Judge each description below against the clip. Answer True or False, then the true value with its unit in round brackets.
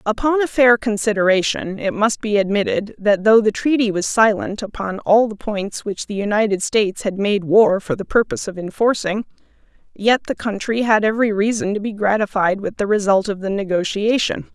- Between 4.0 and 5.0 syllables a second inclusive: False (5.3 syllables/s)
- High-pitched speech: True (210 Hz)